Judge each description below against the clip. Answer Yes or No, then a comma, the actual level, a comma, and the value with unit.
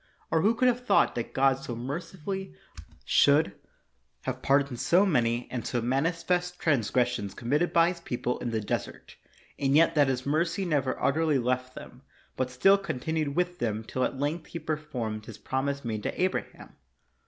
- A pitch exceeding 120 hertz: Yes, medium, 140 Hz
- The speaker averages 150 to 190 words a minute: Yes, average, 170 wpm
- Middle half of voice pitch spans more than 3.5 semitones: Yes, average, 5.2 semitones